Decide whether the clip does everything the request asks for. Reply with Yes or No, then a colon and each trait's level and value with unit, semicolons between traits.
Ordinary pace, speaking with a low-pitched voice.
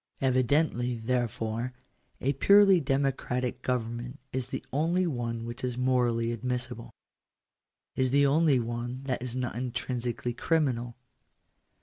No: slow, 120 wpm; low, 125 Hz